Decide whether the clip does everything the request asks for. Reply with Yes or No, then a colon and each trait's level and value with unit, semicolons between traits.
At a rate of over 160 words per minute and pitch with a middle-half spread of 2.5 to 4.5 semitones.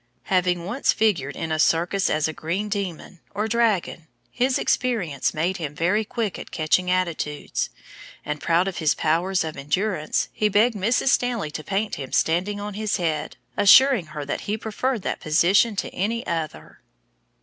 No: average, 170 wpm; average, 4.9 semitones